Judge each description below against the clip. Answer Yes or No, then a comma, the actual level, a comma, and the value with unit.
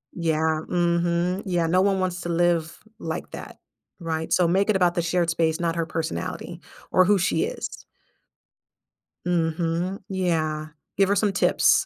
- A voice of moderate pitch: Yes, medium, 175 Hz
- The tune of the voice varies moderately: No, narrow, 2.0 semitones